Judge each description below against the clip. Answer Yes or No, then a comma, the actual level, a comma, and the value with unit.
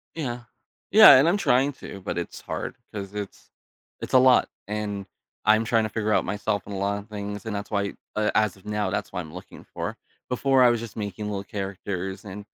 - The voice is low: Yes, low, 105 Hz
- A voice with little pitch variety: Yes, narrow, 2.1 semitones